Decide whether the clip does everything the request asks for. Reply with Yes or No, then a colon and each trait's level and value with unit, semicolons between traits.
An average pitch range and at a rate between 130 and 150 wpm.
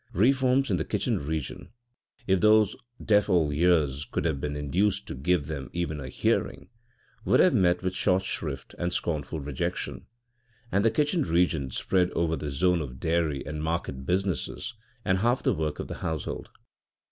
No: average, 4.5 semitones; average, 170 wpm